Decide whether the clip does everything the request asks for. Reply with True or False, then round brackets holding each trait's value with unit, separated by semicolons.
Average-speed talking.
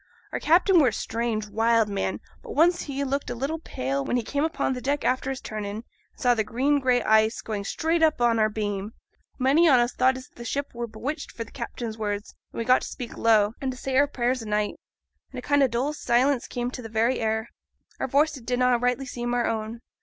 False (240 wpm)